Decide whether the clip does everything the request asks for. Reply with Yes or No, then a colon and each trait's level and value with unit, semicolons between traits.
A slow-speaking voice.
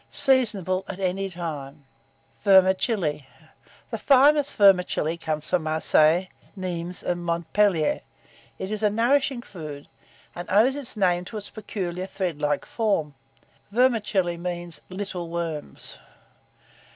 Yes: slow, 115 wpm